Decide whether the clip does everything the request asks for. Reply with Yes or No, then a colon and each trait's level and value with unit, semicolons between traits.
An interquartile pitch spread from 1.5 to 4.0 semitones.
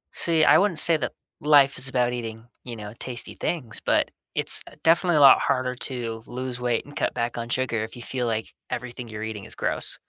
Yes: average, 2.9 semitones